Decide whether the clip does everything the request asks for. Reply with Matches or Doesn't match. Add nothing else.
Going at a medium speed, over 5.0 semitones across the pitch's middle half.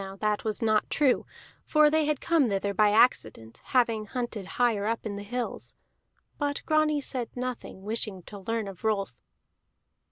Doesn't match